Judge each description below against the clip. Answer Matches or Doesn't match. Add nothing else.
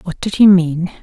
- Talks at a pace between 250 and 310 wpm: Doesn't match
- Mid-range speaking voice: Matches